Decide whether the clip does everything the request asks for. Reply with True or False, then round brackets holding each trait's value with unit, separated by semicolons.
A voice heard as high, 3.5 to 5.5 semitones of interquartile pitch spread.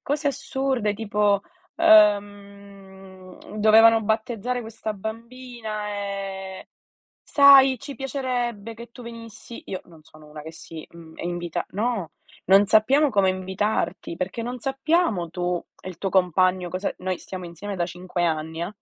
True (205 Hz; 4.1 semitones)